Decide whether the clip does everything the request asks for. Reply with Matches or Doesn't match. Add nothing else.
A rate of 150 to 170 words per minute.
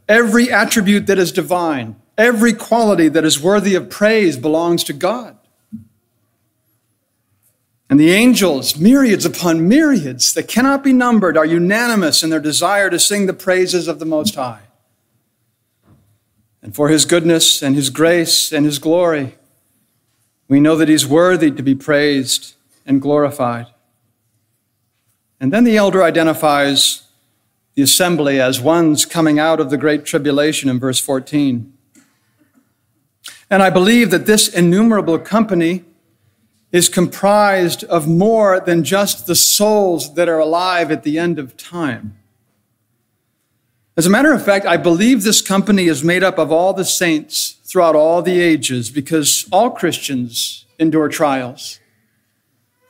Doesn't match